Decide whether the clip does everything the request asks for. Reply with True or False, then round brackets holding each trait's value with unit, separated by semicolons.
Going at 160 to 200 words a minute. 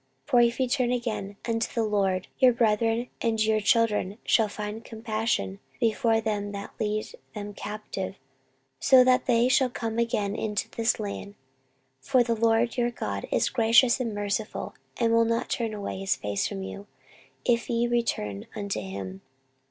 True (165 wpm)